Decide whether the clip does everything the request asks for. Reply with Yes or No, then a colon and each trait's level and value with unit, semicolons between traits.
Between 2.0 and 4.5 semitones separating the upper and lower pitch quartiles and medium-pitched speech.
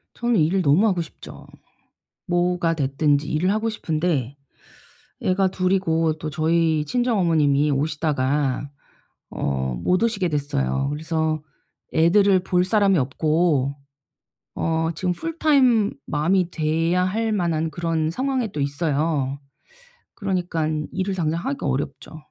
Yes: average, 3.8 semitones; medium, 165 Hz